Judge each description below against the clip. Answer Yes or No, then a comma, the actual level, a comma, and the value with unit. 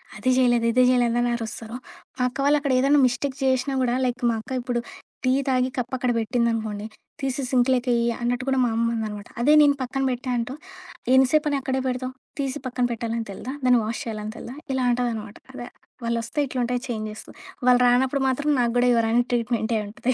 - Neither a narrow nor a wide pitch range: No, narrow, 1.9 semitones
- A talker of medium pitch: No, high, 245 Hz